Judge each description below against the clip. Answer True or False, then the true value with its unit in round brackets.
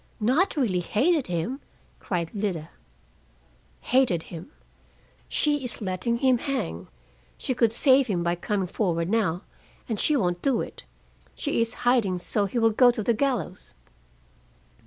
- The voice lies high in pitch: True (220 Hz)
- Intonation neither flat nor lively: False (6.2 semitones)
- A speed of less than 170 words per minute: True (145 wpm)